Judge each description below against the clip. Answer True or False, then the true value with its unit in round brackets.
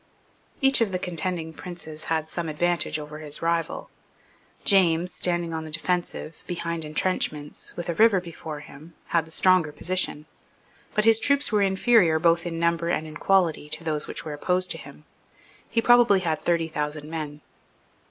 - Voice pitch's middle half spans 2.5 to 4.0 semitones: True (2.8 semitones)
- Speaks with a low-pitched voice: False (170 Hz)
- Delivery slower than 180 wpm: True (170 wpm)